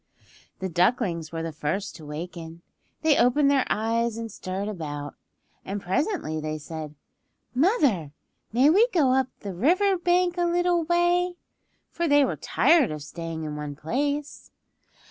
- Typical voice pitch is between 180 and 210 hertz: No, high, 225 Hz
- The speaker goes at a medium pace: Yes, average, 150 wpm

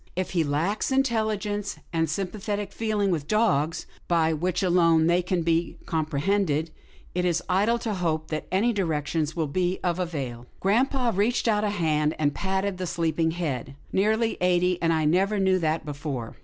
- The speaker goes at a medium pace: Yes, average, 185 wpm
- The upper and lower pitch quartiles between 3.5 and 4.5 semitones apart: Yes, average, 4.2 semitones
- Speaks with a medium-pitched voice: Yes, medium, 175 Hz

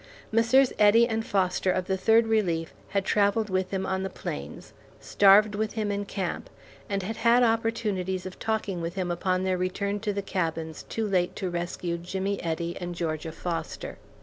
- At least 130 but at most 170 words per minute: No, average, 180 wpm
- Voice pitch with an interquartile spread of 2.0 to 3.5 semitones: Yes, average, 3.1 semitones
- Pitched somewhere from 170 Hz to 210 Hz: Yes, high, 190 Hz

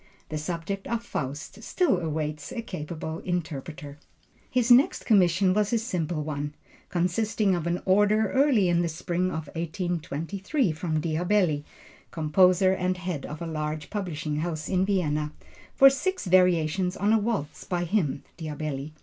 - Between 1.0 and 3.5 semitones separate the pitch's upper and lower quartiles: No, average, 4.2 semitones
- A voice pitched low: No, medium, 175 Hz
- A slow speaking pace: No, average, 150 wpm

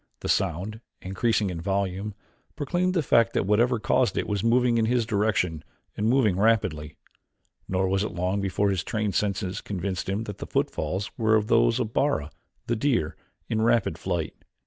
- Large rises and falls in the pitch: No, average, 3.5 semitones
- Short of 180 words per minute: Yes, average, 170 wpm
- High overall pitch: No, low, 105 Hz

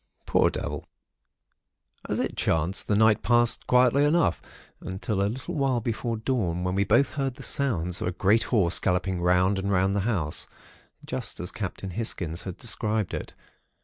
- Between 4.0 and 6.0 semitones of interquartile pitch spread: Yes, average, 4.6 semitones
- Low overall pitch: Yes, low, 100 Hz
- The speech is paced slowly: No, average, 175 wpm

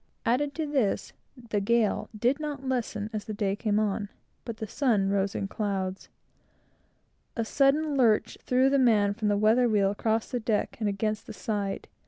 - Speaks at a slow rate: No, average, 180 wpm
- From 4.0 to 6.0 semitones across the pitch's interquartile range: No, average, 3.6 semitones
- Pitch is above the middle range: Yes, high, 220 Hz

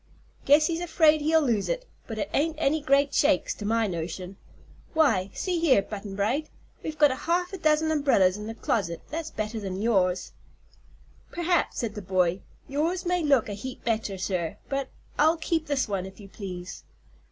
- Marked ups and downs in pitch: Yes, wide, 7.9 semitones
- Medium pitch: No, very high, 260 Hz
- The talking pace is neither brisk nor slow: Yes, average, 180 wpm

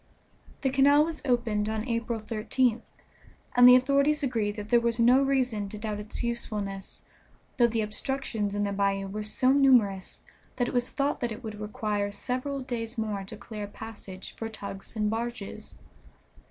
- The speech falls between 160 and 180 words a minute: Yes, average, 175 wpm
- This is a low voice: No, high, 225 Hz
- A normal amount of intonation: Yes, average, 3.1 semitones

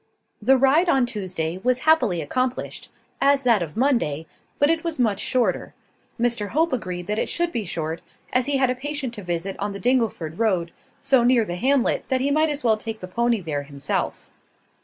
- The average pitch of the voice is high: Yes, high, 235 Hz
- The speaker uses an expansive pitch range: Yes, wide, 6.5 semitones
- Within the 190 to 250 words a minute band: Yes, average, 200 wpm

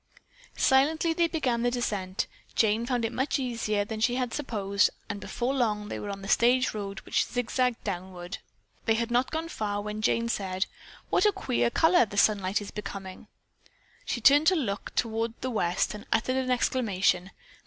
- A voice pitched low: No, high, 225 Hz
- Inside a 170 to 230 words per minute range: Yes, average, 180 wpm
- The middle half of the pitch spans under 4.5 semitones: Yes, average, 3.9 semitones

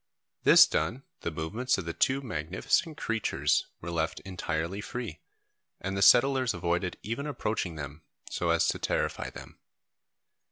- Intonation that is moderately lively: No, wide, 6.6 semitones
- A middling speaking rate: Yes, average, 145 wpm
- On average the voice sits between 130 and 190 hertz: No, very low, 95 Hz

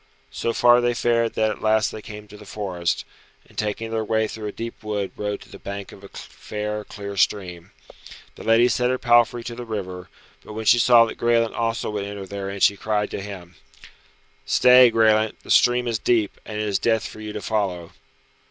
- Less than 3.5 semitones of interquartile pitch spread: Yes, narrow, 2.4 semitones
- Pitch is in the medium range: No, low, 110 Hz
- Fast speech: Yes, fast, 210 wpm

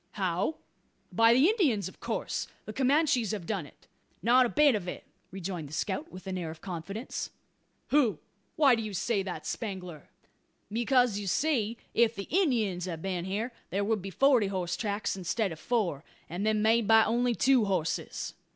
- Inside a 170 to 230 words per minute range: Yes, average, 185 wpm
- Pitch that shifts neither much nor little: Yes, average, 4.5 semitones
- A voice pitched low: No, high, 210 Hz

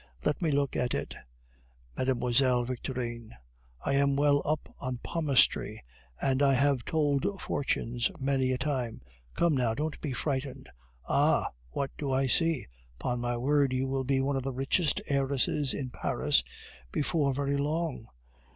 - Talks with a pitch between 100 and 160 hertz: Yes, low, 135 Hz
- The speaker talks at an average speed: Yes, average, 150 wpm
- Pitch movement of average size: No, narrow, 2.1 semitones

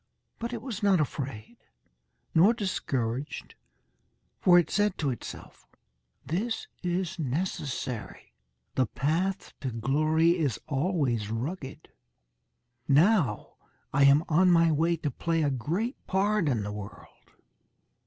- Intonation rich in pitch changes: Yes, wide, 5.8 semitones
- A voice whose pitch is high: No, medium, 155 Hz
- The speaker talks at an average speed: No, slow, 120 wpm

